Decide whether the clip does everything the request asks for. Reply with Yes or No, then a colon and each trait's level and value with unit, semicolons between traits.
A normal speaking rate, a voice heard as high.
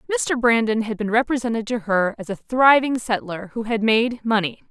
Yes: average, 190 wpm; high, 230 Hz